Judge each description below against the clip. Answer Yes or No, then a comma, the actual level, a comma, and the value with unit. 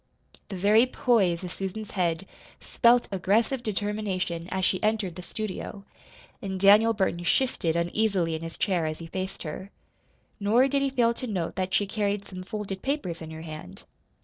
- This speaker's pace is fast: No, average, 175 wpm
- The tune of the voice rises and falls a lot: No, average, 3.6 semitones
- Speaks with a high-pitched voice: Yes, high, 195 Hz